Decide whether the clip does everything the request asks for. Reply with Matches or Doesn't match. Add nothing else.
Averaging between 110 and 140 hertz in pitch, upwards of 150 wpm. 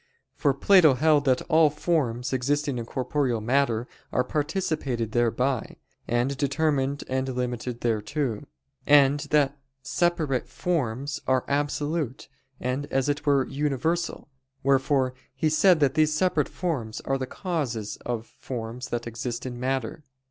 Doesn't match